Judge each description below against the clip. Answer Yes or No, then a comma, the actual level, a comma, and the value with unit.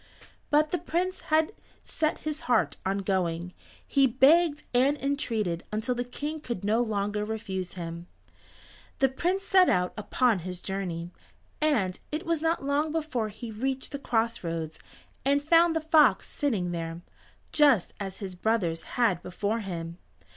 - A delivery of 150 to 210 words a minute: Yes, average, 155 wpm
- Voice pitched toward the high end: Yes, high, 230 Hz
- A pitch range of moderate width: No, wide, 8.0 semitones